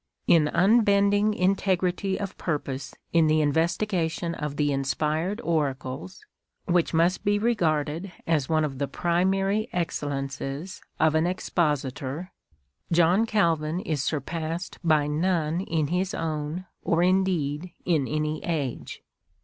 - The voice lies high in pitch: No, medium, 165 Hz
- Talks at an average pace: No, slow, 125 wpm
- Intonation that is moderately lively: Yes, average, 3.7 semitones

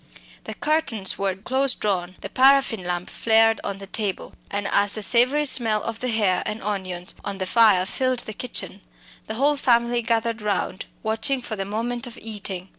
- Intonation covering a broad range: No, average, 3.5 semitones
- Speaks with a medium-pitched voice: No, high, 220 Hz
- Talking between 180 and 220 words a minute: Yes, average, 185 wpm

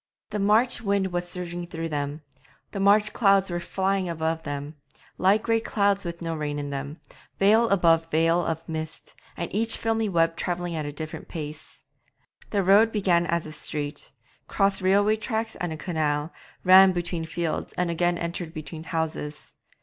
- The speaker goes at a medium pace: Yes, average, 170 wpm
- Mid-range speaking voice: Yes, medium, 175 Hz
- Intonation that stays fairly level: No, average, 3.7 semitones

